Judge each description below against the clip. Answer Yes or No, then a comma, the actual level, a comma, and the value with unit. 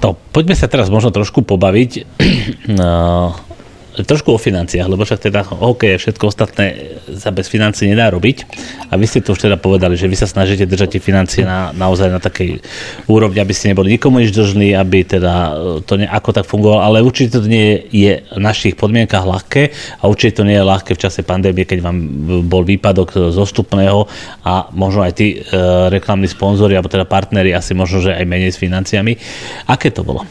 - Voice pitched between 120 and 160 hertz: No, low, 100 Hz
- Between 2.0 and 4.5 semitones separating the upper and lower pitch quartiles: Yes, narrow, 2.5 semitones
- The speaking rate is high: Yes, fast, 195 wpm